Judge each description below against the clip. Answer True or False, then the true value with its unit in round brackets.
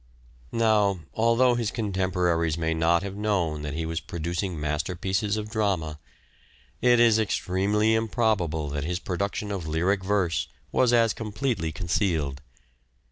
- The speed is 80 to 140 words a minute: True (135 wpm)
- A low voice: True (95 Hz)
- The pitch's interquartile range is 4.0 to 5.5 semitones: True (4.7 semitones)